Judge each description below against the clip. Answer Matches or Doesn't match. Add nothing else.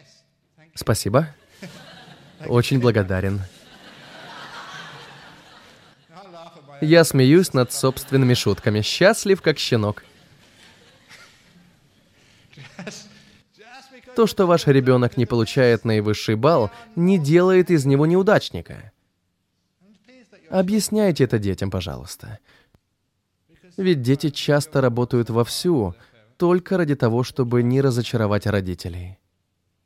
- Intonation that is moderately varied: Doesn't match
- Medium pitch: Doesn't match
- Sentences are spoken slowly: Matches